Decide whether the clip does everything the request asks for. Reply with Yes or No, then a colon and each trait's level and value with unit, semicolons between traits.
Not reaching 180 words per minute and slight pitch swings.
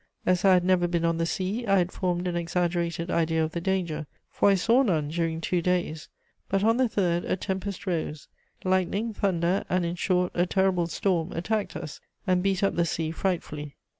No: average, 200 wpm; narrow, 2.3 semitones